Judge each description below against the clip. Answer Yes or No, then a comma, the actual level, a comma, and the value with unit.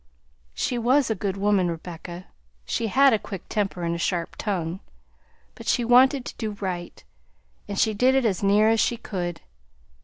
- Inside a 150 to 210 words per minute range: Yes, average, 180 wpm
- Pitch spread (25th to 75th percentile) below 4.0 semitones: No, average, 4.7 semitones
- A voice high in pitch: Yes, high, 205 Hz